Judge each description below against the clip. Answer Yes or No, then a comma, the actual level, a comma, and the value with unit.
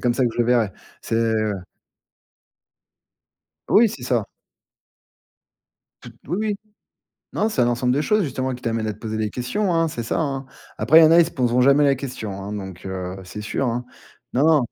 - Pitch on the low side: Yes, low, 125 Hz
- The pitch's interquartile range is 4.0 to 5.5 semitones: Yes, average, 4.7 semitones